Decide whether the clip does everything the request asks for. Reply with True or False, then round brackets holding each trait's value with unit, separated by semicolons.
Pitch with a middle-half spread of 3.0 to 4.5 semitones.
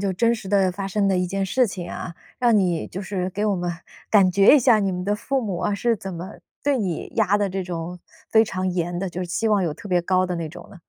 False (2.5 semitones)